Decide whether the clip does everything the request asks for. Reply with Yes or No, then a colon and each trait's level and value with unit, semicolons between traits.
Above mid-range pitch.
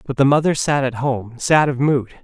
No: low, 135 Hz